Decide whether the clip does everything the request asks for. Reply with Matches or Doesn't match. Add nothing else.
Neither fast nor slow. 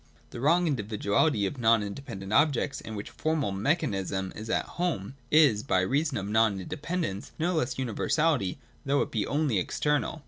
Matches